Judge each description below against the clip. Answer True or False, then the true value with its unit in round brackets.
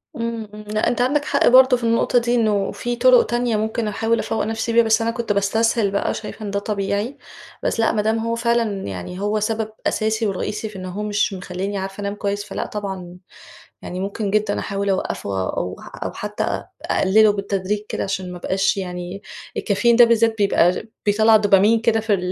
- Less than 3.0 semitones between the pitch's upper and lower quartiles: True (2.5 semitones)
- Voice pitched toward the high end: True (210 Hz)